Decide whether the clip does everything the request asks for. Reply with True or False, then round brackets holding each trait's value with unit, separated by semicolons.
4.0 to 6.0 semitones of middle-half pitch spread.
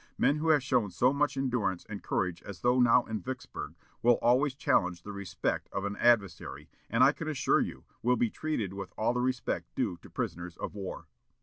True (4.8 semitones)